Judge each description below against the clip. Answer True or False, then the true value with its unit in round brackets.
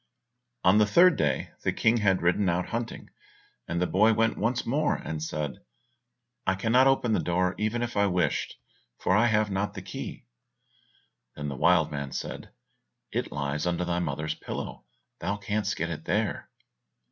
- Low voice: True (95 Hz)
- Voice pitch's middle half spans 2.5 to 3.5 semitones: False (4.7 semitones)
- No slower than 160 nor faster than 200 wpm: True (170 wpm)